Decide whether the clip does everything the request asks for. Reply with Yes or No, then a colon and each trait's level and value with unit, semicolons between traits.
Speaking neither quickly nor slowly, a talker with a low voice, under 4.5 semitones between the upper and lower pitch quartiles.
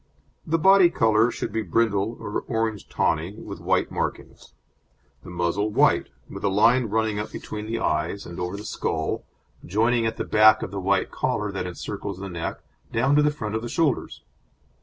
Yes: average, 180 wpm; low, 110 Hz; average, 2.8 semitones